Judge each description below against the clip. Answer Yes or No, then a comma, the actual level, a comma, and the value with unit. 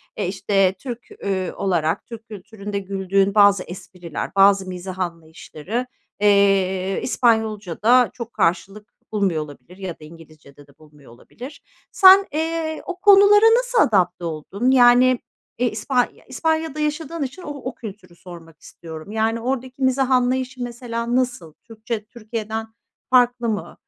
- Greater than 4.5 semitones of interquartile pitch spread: Yes, wide, 5.5 semitones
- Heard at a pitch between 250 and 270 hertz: No, high, 215 Hz